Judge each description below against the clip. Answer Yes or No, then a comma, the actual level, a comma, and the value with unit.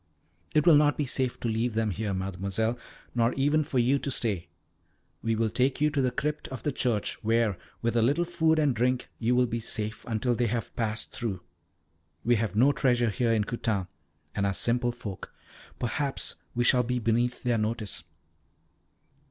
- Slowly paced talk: No, average, 185 wpm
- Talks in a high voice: No, low, 120 Hz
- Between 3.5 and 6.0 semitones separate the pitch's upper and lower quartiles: No, average, 2.8 semitones